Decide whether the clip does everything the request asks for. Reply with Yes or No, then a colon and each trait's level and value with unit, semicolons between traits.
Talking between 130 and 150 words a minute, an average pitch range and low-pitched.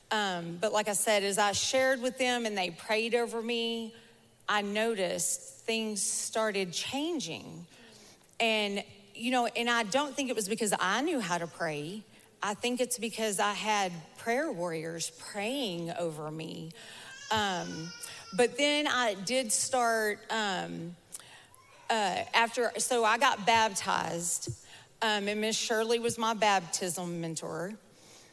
No: average, 140 wpm; average, 4.5 semitones; high, 215 Hz